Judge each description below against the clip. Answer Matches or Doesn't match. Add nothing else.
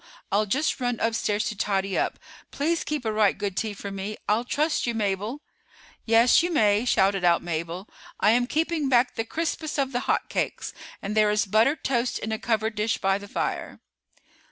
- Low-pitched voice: Doesn't match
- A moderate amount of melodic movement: Matches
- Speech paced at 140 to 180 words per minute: Doesn't match